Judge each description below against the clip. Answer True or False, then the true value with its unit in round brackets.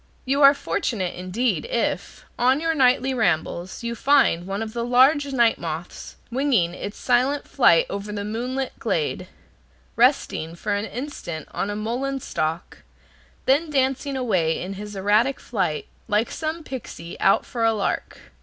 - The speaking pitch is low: False (235 Hz)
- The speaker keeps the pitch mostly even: False (5.5 semitones)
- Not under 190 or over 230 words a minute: False (155 wpm)